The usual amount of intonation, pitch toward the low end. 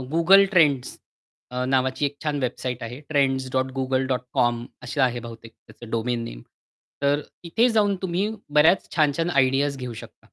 Yes: average, 3.2 semitones; low, 130 Hz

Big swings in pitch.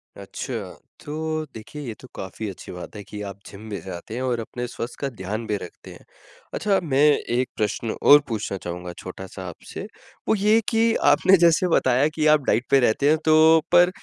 Yes: wide, 7.2 semitones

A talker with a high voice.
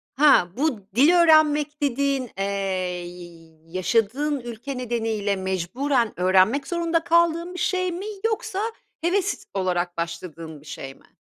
Yes: very high, 250 Hz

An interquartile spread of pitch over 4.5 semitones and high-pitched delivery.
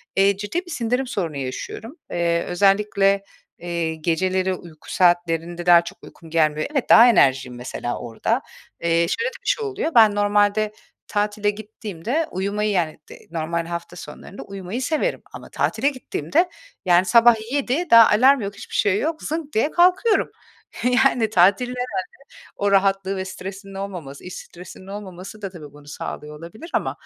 Yes: average, 5.2 semitones; high, 195 Hz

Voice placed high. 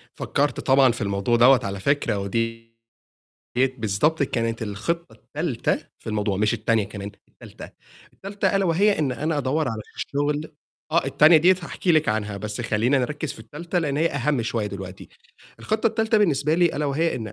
No: low, 135 Hz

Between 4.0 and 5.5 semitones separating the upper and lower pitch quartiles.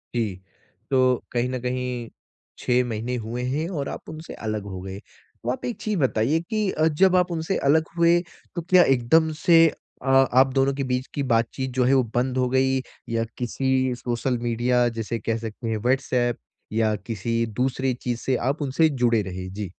No: average, 2.8 semitones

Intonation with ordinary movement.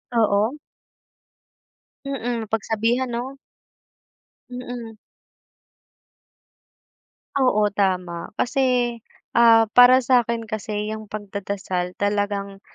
Yes: average, 3.3 semitones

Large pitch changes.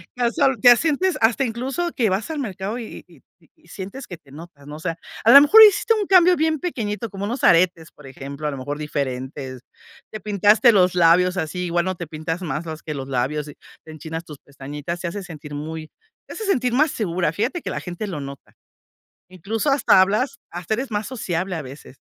Yes: wide, 7.5 semitones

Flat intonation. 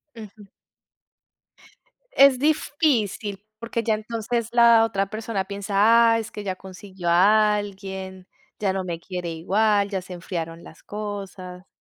No: average, 3.0 semitones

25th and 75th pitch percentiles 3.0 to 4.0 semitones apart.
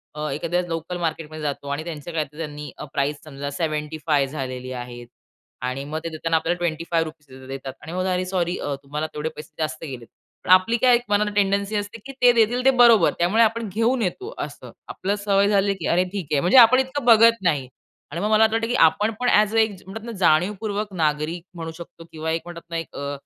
No: wide, 5.5 semitones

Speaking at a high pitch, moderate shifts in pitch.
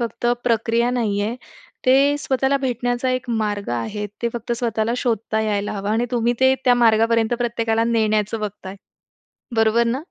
No: high, 230 Hz; narrow, 2.1 semitones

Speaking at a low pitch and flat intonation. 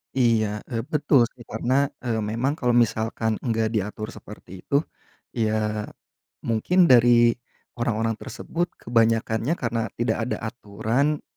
Yes: low, 115 Hz; narrow, 2.3 semitones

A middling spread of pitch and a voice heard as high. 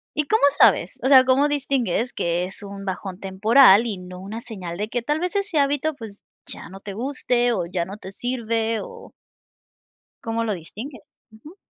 No: wide, 5.8 semitones; high, 225 Hz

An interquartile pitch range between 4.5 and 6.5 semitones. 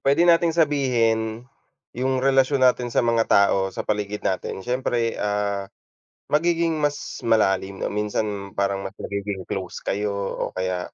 Yes: average, 5.0 semitones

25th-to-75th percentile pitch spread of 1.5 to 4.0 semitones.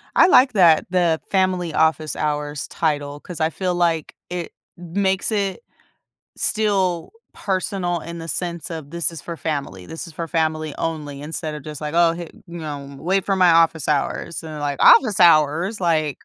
Yes: average, 2.7 semitones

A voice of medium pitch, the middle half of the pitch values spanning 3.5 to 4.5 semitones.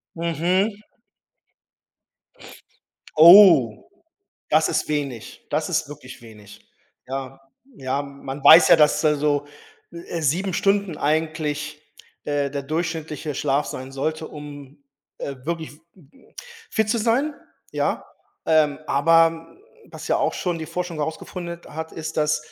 No: medium, 155 Hz; average, 2.9 semitones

